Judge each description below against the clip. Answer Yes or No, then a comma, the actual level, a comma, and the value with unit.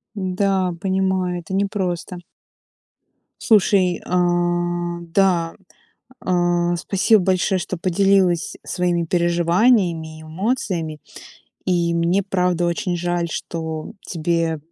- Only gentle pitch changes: Yes, narrow, 1.8 semitones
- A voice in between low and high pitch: Yes, medium, 175 Hz